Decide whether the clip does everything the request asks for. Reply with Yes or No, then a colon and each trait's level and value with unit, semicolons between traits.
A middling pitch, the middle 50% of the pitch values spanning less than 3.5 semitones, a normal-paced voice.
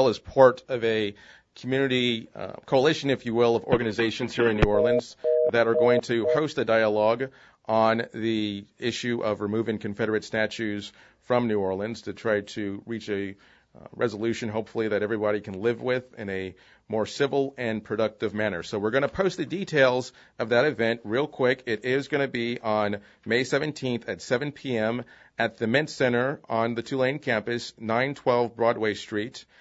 No: low, 115 Hz; average, 2.8 semitones; average, 175 wpm